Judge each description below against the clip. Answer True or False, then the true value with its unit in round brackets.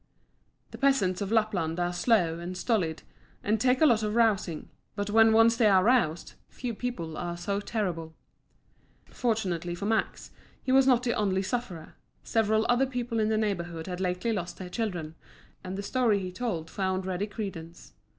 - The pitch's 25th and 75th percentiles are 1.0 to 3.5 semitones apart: False (4.4 semitones)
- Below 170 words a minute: False (175 wpm)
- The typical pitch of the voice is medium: False (205 Hz)